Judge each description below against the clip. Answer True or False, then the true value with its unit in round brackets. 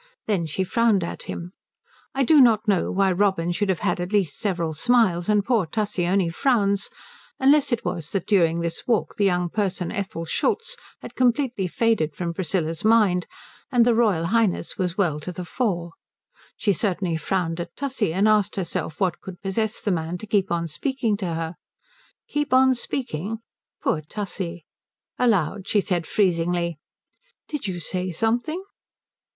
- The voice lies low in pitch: False (190 Hz)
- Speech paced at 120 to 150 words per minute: False (170 wpm)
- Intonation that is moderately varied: True (4.6 semitones)